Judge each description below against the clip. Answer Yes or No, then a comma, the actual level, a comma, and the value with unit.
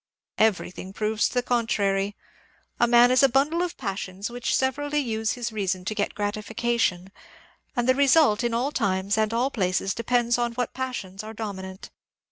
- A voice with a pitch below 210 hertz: No, high, 225 Hz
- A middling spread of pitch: Yes, average, 3.7 semitones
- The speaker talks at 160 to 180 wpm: Yes, average, 165 wpm